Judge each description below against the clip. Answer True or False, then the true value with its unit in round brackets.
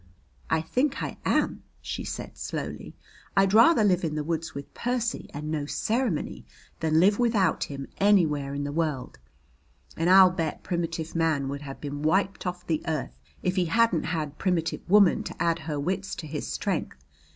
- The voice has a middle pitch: True (165 Hz)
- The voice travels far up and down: False (4.1 semitones)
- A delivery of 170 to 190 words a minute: True (175 wpm)